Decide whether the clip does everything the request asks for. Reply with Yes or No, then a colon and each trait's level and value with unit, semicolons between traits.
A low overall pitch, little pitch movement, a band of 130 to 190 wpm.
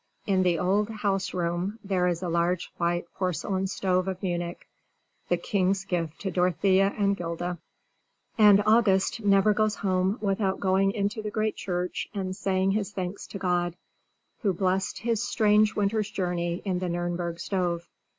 No: high, 190 Hz; narrow, 2.3 semitones; average, 160 wpm